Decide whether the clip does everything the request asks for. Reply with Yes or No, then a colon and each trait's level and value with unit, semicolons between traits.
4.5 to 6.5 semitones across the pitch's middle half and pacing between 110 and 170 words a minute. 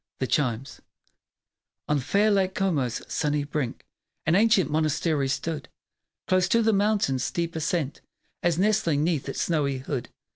Yes: average, 5.1 semitones; average, 140 wpm